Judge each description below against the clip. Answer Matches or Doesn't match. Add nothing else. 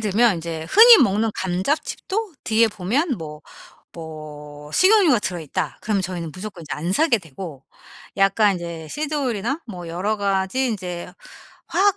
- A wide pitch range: Matches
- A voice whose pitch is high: Matches